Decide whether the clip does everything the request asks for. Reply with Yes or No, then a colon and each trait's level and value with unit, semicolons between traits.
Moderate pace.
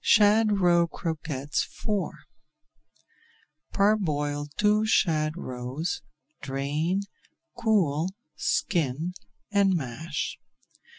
No: slow, 70 wpm